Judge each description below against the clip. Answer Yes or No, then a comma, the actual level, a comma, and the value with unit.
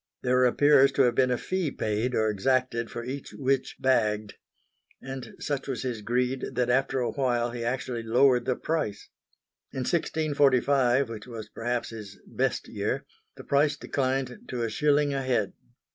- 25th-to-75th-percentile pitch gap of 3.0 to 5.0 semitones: No, narrow, 2.6 semitones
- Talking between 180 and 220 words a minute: No, average, 165 wpm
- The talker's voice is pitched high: No, low, 125 Hz